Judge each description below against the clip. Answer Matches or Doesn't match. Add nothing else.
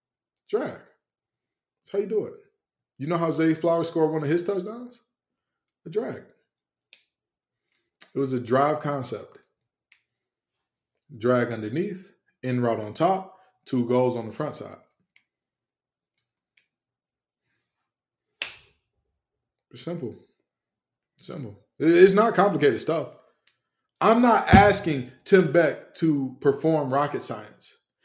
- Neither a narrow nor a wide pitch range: Doesn't match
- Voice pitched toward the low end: Doesn't match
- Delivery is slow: Matches